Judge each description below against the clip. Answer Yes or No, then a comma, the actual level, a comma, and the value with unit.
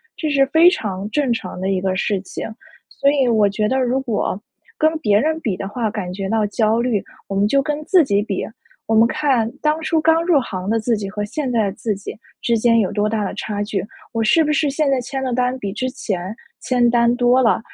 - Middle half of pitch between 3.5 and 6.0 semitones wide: Yes, average, 4.7 semitones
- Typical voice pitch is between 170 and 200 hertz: No, high, 230 Hz